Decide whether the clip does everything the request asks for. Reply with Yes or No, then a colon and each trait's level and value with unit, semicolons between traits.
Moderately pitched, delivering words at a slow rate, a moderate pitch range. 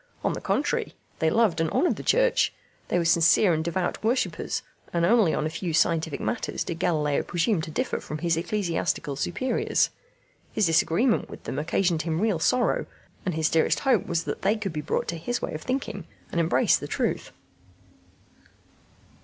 No: medium, 170 Hz; average, 180 wpm; average, 4.6 semitones